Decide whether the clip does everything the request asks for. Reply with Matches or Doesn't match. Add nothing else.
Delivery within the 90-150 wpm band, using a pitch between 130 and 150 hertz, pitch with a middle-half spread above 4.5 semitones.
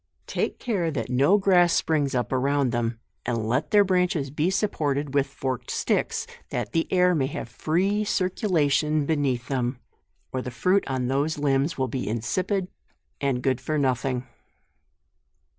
Doesn't match